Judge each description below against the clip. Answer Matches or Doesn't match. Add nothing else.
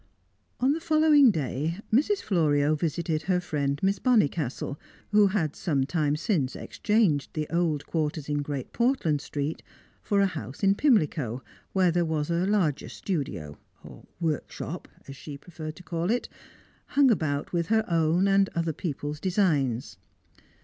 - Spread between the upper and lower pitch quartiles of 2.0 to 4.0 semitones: Doesn't match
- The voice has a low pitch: Doesn't match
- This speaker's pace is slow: Doesn't match